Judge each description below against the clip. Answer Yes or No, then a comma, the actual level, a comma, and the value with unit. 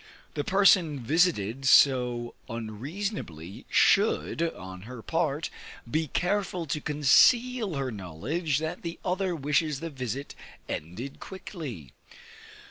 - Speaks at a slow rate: Yes, slow, 110 wpm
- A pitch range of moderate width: No, wide, 6.6 semitones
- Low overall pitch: No, medium, 145 Hz